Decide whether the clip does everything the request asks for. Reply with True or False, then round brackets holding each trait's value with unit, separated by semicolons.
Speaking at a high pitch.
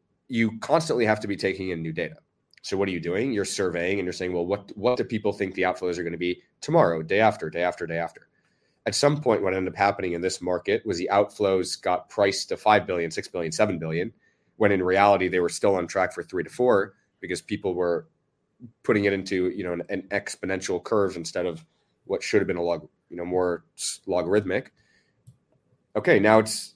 False (95 Hz)